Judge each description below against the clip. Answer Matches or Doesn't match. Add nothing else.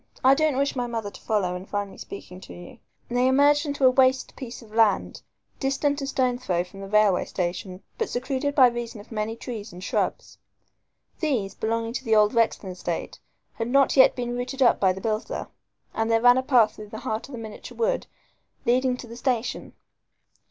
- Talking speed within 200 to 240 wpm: Matches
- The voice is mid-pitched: Doesn't match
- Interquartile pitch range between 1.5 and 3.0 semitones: Doesn't match